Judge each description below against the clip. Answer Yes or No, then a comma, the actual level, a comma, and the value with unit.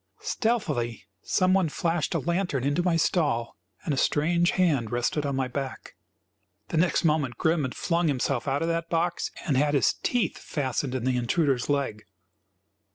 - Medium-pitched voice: Yes, medium, 150 Hz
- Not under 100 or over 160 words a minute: No, average, 170 wpm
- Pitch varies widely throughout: No, average, 4.6 semitones